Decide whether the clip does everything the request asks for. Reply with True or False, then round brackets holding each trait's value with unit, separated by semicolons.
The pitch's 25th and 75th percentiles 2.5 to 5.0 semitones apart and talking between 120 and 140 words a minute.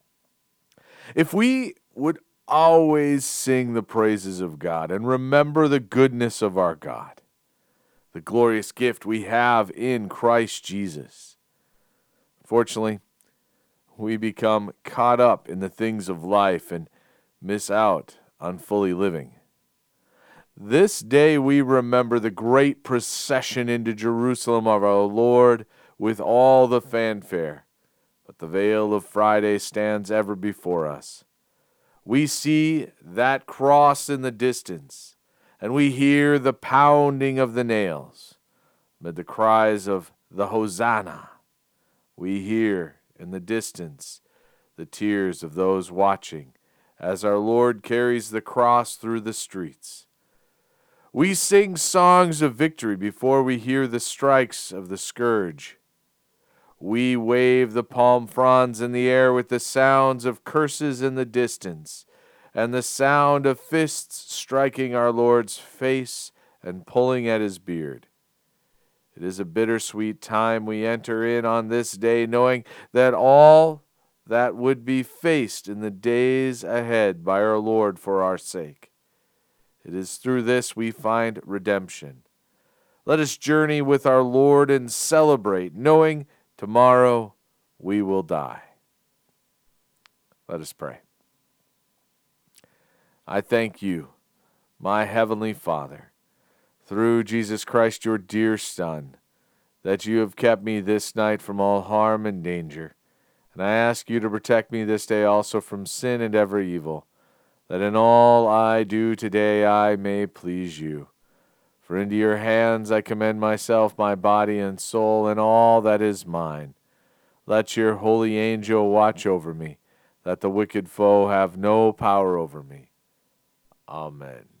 True (3.7 semitones; 135 wpm)